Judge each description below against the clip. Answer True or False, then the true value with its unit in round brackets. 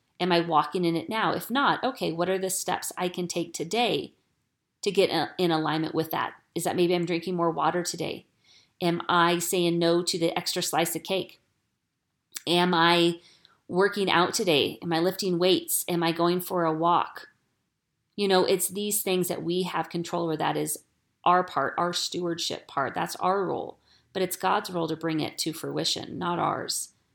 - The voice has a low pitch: False (175 Hz)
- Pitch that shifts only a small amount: True (1.5 semitones)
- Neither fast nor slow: True (190 wpm)